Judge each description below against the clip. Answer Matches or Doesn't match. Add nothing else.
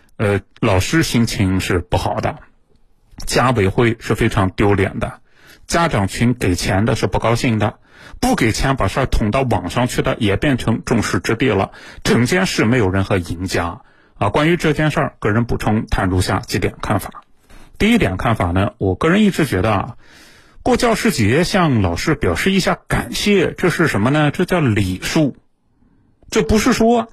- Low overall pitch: Matches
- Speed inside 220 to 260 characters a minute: Matches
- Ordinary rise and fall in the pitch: Doesn't match